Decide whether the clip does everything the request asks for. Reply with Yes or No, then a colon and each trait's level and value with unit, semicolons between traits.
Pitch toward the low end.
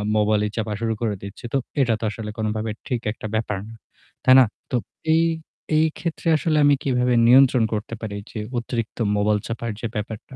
Yes: low, 115 Hz